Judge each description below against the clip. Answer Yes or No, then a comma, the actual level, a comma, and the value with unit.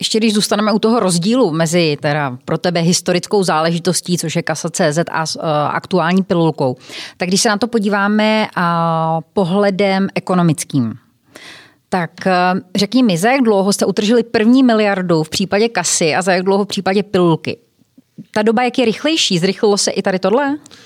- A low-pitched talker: No, high, 190 Hz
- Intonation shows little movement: No, average, 4.1 semitones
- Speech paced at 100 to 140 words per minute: No, average, 165 wpm